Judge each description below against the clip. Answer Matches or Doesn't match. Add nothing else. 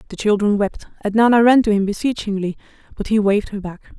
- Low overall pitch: Doesn't match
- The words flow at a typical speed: Doesn't match